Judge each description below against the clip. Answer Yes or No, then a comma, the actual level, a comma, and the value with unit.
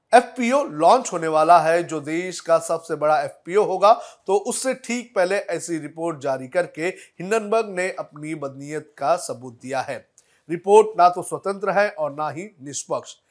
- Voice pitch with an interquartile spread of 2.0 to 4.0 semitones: No, average, 4.8 semitones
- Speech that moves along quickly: No, average, 165 wpm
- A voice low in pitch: No, medium, 175 Hz